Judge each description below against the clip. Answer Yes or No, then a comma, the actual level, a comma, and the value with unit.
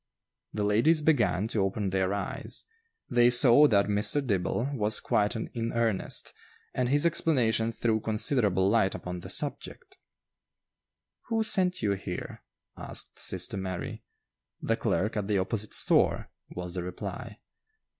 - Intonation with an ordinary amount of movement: Yes, average, 4.2 semitones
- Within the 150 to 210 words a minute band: No, slow, 135 wpm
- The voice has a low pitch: Yes, low, 110 Hz